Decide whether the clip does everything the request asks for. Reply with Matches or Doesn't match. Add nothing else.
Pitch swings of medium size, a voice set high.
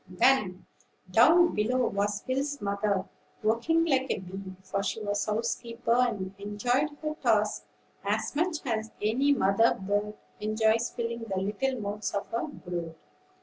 Matches